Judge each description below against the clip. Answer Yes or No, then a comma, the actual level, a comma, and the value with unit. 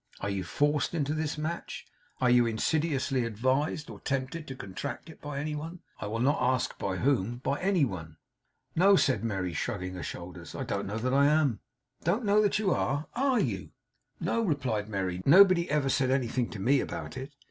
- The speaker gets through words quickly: No, average, 195 wpm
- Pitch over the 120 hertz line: Yes, low, 135 Hz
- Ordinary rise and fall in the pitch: No, wide, 5.9 semitones